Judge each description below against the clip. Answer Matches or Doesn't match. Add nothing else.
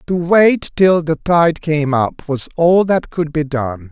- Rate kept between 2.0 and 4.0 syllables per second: Matches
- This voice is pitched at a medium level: Matches